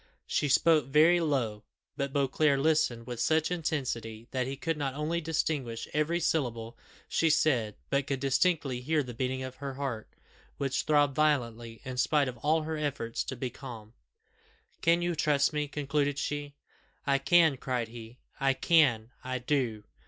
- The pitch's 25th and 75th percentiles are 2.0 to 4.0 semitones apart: Yes, average, 3.6 semitones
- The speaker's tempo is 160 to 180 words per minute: Yes, average, 165 wpm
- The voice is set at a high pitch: No, medium, 140 Hz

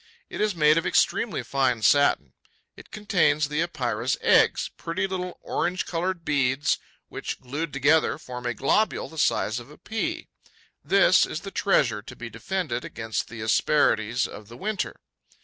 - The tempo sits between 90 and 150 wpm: No, average, 160 wpm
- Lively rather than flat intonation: Yes, wide, 6.9 semitones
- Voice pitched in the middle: Yes, medium, 150 Hz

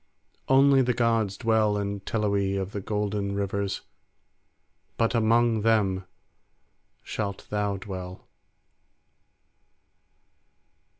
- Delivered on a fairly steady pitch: Yes, narrow, 2.3 semitones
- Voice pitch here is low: Yes, low, 105 Hz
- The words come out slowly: Yes, slow, 85 wpm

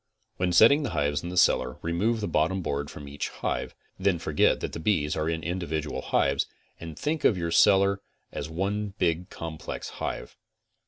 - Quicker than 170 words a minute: Yes, average, 180 wpm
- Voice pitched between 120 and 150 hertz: No, very low, 85 Hz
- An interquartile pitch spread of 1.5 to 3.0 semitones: No, average, 4.1 semitones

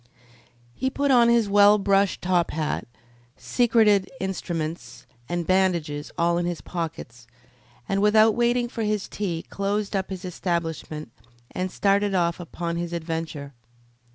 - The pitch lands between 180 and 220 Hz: Yes, medium, 185 Hz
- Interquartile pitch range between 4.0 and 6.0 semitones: No, average, 3.6 semitones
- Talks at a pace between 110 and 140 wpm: Yes, slow, 135 wpm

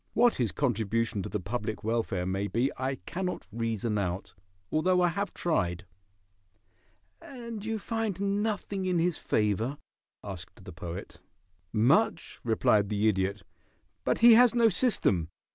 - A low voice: Yes, low, 120 Hz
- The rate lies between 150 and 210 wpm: No, average, 140 wpm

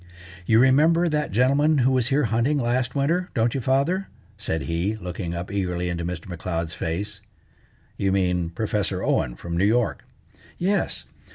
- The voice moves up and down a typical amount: No, wide, 7.5 semitones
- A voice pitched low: Yes, low, 110 Hz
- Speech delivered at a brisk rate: No, average, 160 wpm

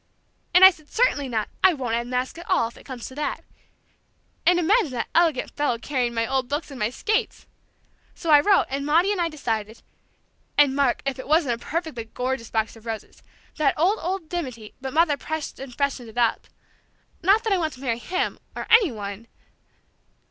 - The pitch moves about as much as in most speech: No, wide, 5.9 semitones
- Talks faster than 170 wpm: Yes, average, 200 wpm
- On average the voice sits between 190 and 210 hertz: No, very high, 280 Hz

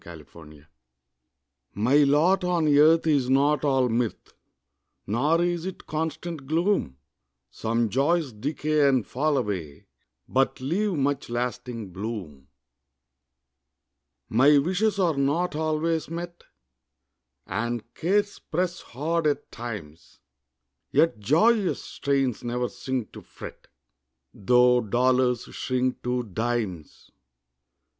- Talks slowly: Yes, slow, 105 wpm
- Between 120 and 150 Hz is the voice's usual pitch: Yes, low, 135 Hz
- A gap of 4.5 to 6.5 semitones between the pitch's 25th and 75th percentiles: Yes, wide, 5.4 semitones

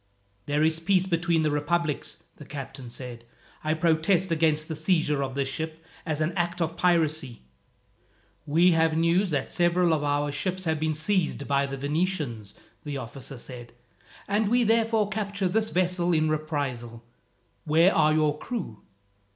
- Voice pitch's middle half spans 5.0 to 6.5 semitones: No, average, 3.5 semitones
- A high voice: No, medium, 160 Hz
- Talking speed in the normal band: Yes, average, 160 wpm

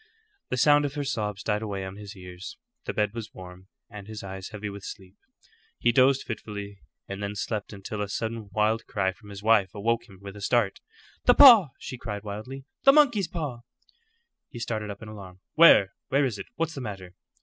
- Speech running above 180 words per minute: Yes, fast, 205 wpm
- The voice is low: Yes, low, 105 Hz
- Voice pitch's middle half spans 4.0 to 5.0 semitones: No, average, 3.3 semitones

